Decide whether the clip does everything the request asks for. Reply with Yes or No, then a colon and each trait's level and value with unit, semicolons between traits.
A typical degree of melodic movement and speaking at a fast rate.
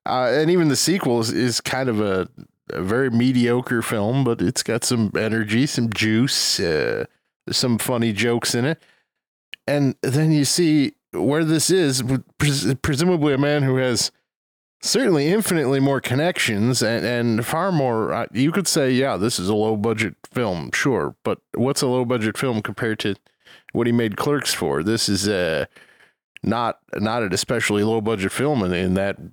No: average, 4.4 semitones; average, 170 wpm